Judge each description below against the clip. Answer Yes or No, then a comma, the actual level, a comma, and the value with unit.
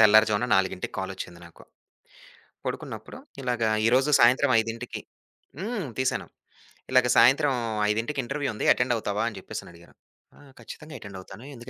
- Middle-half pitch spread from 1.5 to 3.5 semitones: No, average, 3.9 semitones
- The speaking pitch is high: No, low, 120 Hz